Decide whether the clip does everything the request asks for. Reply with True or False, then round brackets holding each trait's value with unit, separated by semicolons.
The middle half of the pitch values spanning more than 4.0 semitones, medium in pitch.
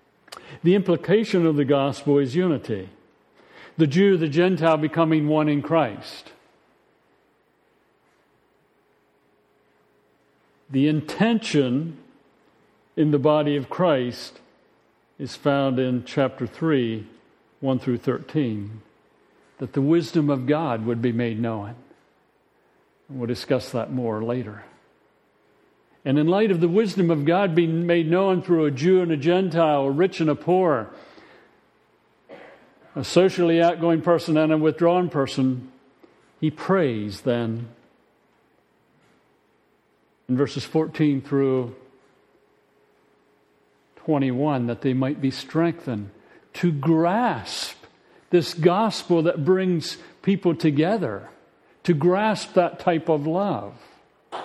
True (4.6 semitones; 155 Hz)